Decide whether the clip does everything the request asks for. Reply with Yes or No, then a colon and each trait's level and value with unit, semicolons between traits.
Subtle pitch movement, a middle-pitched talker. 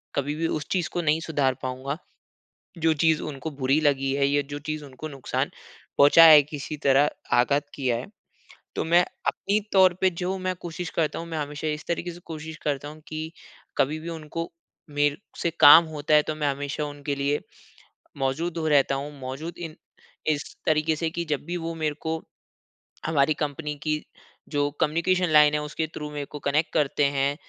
Yes: narrow, 2.1 semitones; medium, 150 Hz